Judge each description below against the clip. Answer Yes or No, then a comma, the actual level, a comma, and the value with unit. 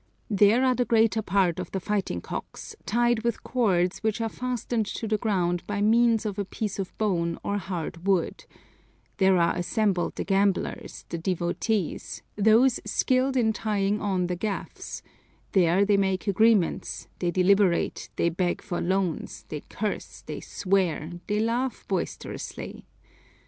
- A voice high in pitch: Yes, high, 200 Hz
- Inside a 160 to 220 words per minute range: No, average, 150 wpm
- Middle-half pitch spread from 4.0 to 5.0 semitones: No, average, 3.4 semitones